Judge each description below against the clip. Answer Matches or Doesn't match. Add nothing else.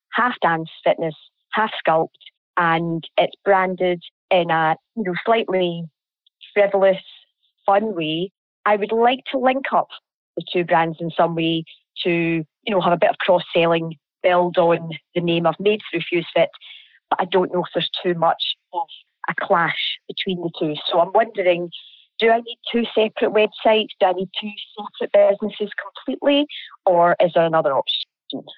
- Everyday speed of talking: Matches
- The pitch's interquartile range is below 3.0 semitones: Doesn't match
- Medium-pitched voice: Matches